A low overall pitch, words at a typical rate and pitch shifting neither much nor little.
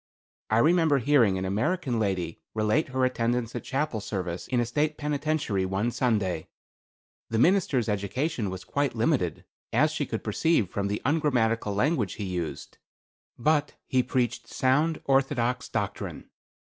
No: low, 120 Hz; average, 145 wpm; wide, 6.0 semitones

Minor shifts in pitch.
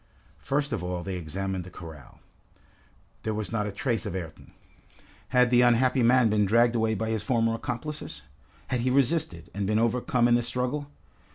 No: average, 3.6 semitones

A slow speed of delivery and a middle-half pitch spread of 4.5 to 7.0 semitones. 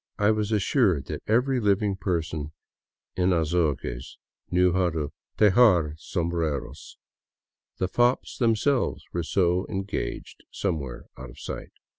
Yes: slow, 120 wpm; average, 4.8 semitones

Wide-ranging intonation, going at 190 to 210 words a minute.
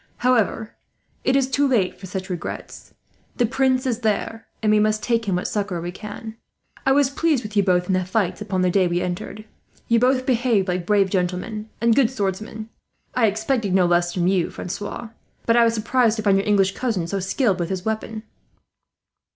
No: average, 3.8 semitones; average, 200 wpm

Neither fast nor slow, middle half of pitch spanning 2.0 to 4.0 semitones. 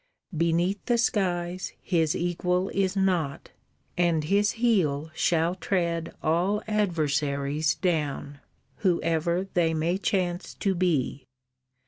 No: slow, 105 wpm; average, 3.0 semitones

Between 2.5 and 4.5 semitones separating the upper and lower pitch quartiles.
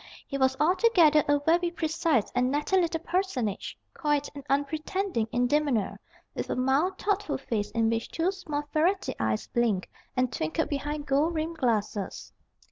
No: average, 5.2 semitones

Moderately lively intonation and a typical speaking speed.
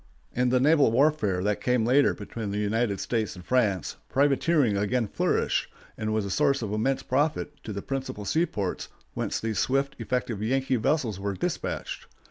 Yes: average, 4.6 semitones; average, 170 wpm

